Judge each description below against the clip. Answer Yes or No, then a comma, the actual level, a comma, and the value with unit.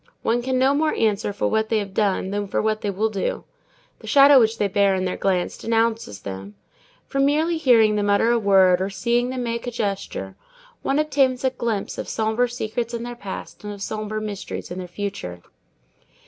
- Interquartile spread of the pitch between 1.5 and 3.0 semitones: No, average, 3.4 semitones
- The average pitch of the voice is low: No, high, 220 Hz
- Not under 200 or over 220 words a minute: Yes, fast, 205 wpm